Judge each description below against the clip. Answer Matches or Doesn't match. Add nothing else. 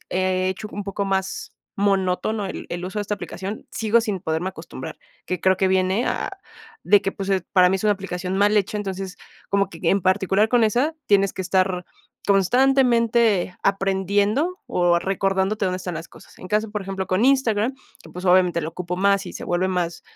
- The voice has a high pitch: Matches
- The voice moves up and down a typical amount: Doesn't match